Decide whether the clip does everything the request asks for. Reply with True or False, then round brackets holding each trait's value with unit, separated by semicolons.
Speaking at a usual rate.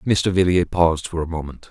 False (210 wpm)